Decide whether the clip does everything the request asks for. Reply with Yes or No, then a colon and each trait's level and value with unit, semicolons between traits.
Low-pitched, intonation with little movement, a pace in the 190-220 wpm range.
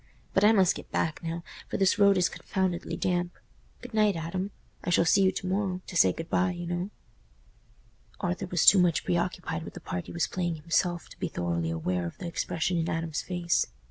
No: medium, 175 Hz; narrow, 2.1 semitones; fast, 205 wpm